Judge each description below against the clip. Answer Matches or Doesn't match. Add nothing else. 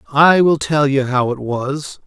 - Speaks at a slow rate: Doesn't match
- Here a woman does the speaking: Doesn't match